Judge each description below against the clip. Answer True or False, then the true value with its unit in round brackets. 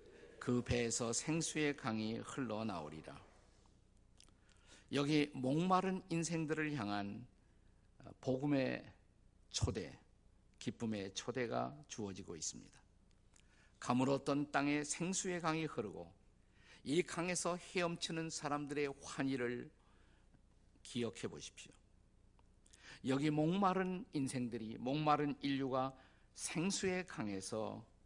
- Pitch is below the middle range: True (125 Hz)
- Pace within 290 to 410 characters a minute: False (220 characters per minute)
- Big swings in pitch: True (7.0 semitones)